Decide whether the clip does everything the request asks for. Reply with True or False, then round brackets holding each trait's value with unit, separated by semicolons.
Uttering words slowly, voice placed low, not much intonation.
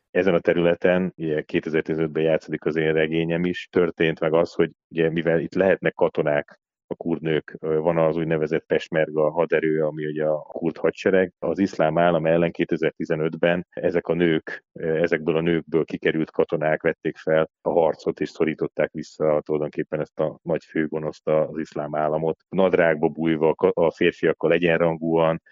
False (150 wpm; 80 Hz; 1.3 semitones)